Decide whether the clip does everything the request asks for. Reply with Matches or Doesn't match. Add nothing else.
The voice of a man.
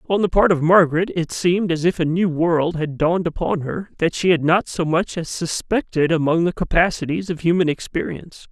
Matches